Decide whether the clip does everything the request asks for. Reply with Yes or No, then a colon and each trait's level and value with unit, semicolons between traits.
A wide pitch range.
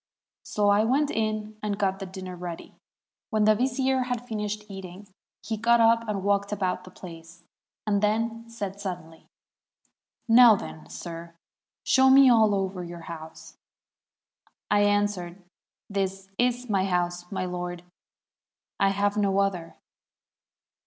No: average, 3.2 semitones